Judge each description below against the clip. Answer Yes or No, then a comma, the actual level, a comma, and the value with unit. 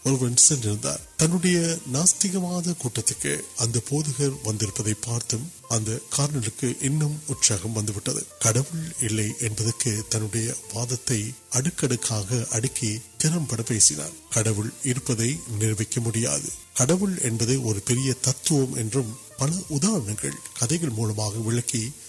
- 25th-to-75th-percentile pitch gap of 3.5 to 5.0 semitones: Yes, average, 4.1 semitones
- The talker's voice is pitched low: Yes, low, 120 Hz